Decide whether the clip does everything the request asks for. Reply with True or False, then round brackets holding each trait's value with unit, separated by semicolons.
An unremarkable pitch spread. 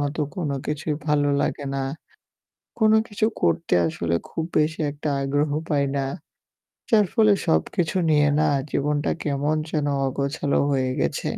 False (2.0 semitones)